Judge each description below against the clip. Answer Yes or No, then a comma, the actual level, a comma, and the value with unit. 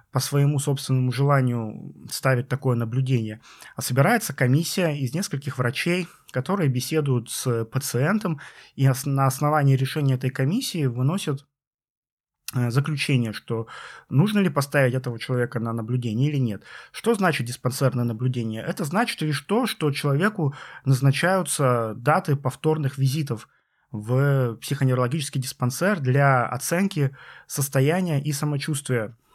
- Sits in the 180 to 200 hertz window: No, low, 135 Hz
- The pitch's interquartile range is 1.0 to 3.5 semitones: Yes, average, 3.2 semitones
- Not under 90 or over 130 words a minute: Yes, average, 115 wpm